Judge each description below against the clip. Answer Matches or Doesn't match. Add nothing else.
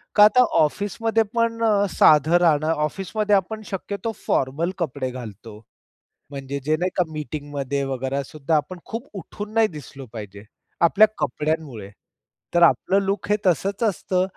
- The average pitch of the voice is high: Doesn't match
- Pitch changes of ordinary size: Doesn't match